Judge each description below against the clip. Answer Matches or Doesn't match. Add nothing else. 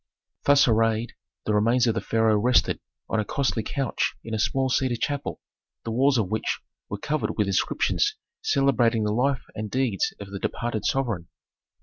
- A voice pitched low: Matches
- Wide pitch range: Doesn't match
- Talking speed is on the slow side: Doesn't match